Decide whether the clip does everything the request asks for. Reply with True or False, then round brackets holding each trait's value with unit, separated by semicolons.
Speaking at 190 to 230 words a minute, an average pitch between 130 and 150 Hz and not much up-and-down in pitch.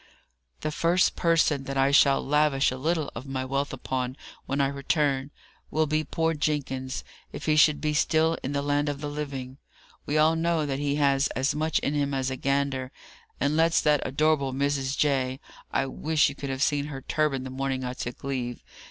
True (200 wpm; 140 Hz; 2.2 semitones)